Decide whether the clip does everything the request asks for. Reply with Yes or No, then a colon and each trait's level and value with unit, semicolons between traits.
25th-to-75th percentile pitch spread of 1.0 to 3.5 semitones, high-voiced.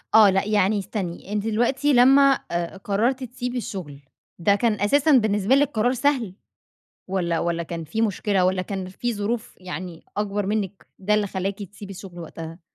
No: average, 3.9 semitones; high, 205 Hz